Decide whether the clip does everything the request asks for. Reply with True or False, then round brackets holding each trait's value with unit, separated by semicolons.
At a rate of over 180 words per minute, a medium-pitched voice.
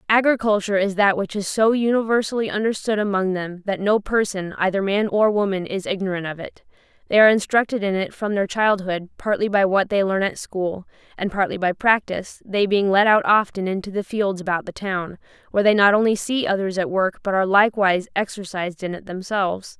False (200 wpm; 200 Hz)